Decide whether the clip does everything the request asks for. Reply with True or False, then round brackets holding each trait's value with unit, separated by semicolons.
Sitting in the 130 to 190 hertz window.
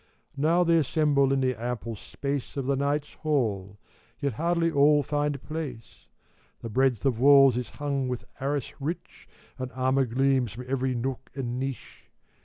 True (135 Hz)